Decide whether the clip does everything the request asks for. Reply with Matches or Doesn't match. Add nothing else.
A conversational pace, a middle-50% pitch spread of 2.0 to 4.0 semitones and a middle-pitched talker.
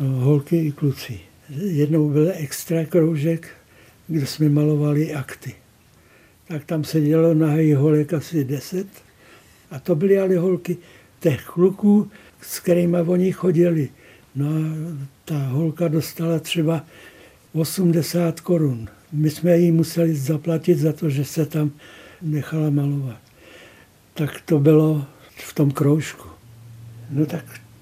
Matches